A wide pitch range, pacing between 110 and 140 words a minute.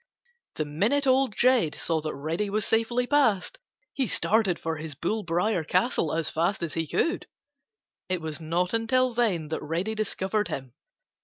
No: wide, 6.0 semitones; average, 165 wpm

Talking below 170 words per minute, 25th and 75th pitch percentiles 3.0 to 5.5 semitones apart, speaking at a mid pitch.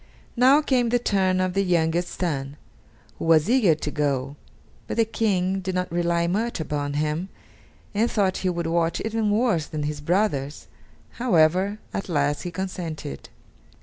Yes: average, 160 wpm; average, 4.7 semitones; medium, 180 Hz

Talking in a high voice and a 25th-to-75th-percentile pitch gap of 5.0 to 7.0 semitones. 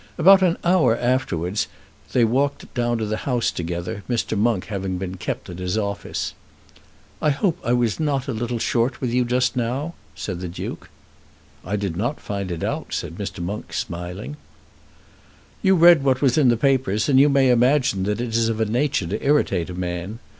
No: low, 115 Hz; wide, 5.6 semitones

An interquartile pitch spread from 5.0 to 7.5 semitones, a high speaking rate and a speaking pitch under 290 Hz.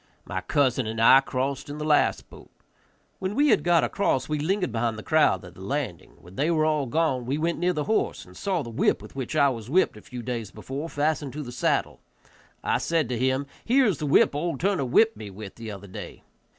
Yes: average, 5.3 semitones; fast, 235 wpm; medium, 140 Hz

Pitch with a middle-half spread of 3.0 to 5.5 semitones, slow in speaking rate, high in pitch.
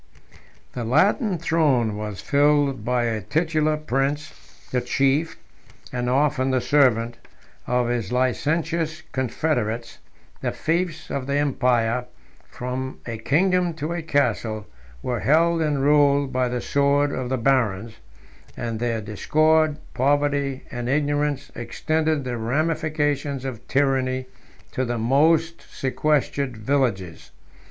No: average, 3.8 semitones; slow, 120 wpm; low, 135 Hz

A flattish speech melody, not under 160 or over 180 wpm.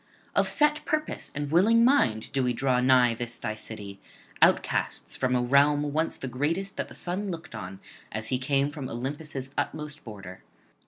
No: average, 4.8 semitones; average, 175 wpm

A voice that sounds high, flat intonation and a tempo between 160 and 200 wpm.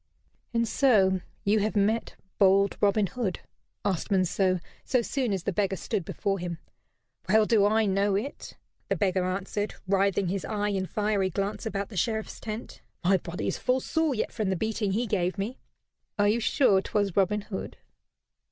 Yes: high, 200 Hz; narrow, 2.3 semitones; average, 175 wpm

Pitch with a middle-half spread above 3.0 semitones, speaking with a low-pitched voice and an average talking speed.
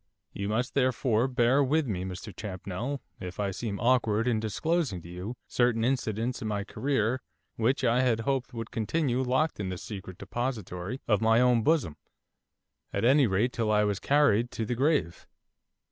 Yes: average, 3.8 semitones; low, 115 Hz; average, 175 wpm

